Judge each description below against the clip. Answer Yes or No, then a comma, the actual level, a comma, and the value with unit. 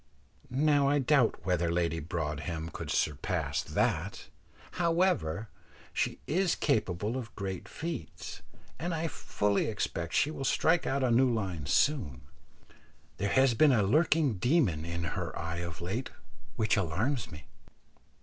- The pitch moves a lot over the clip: Yes, wide, 9.0 semitones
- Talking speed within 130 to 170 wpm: Yes, average, 140 wpm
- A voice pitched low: Yes, low, 110 Hz